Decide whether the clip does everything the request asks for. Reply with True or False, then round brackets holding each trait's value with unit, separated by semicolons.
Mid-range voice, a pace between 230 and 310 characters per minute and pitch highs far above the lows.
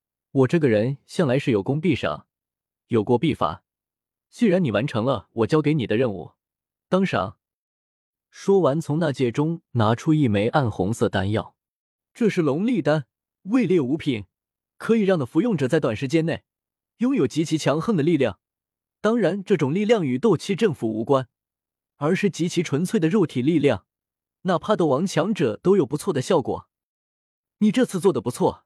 True (155 Hz; 250 characters per minute; 7.1 semitones)